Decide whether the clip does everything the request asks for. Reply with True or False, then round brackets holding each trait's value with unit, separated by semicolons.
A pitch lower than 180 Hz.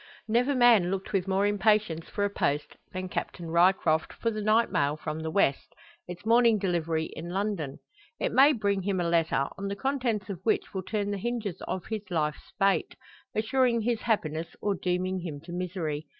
False (195 Hz)